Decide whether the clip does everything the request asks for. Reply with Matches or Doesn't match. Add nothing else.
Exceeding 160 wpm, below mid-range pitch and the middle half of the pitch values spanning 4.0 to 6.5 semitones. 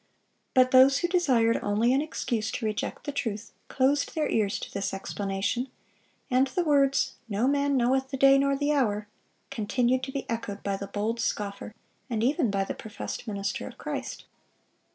Doesn't match